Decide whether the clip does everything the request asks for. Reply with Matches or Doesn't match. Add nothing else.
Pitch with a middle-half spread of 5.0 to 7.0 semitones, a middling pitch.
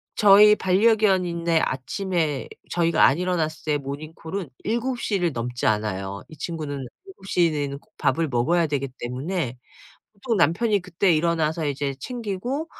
Matches